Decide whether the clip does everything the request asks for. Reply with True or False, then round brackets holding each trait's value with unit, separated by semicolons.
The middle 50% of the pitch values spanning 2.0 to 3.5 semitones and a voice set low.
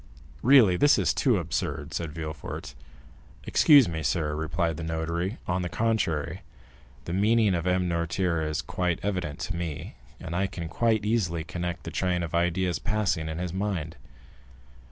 True (2.9 semitones; 85 Hz)